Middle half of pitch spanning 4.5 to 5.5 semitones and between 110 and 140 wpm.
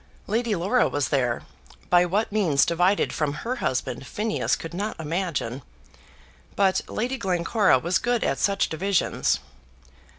Yes: average, 4.9 semitones; slow, 135 wpm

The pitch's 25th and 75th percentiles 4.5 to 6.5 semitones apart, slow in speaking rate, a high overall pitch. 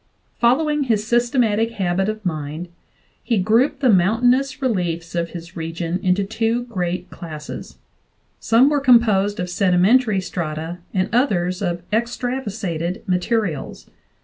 Yes: average, 5.2 semitones; slow, 125 wpm; high, 200 Hz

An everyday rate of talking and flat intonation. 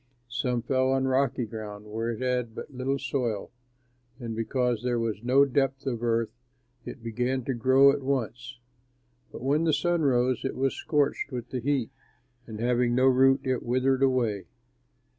Yes: average, 170 wpm; narrow, 2.2 semitones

